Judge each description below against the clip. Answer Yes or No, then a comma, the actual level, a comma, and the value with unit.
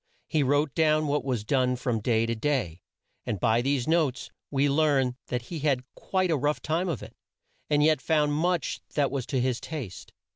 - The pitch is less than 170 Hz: Yes, medium, 140 Hz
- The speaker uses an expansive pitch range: No, average, 3.8 semitones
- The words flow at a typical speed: Yes, average, 195 wpm